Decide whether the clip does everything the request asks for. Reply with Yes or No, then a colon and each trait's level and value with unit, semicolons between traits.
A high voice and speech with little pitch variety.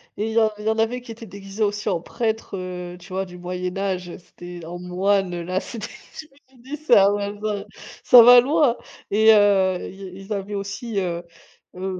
No: high, 200 Hz; average, 3.3 semitones